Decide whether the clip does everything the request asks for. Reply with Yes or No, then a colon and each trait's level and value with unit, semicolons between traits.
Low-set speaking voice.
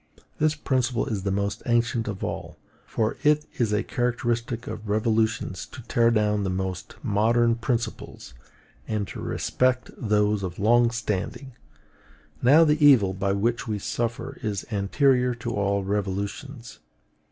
Yes: low, 115 Hz